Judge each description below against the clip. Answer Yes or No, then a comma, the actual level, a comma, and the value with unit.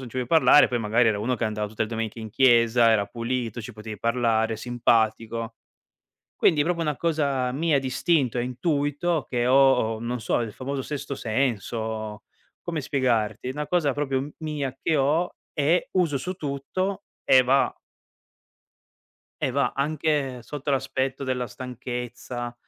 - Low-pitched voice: Yes, low, 130 Hz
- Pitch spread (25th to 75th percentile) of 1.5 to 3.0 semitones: No, average, 3.8 semitones